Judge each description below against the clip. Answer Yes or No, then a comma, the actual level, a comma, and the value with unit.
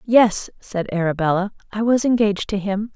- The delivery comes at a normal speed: Yes, average, 165 wpm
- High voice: Yes, high, 205 Hz